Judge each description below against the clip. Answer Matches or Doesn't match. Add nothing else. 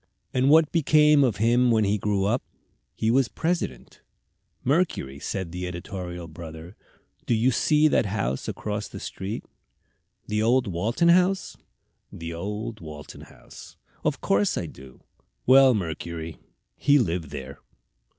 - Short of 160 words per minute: Matches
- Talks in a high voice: Doesn't match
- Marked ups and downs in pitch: Matches